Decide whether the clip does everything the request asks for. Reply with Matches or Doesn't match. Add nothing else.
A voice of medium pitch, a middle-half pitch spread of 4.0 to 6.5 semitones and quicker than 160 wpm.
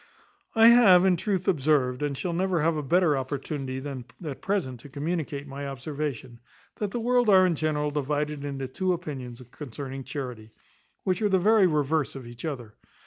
Matches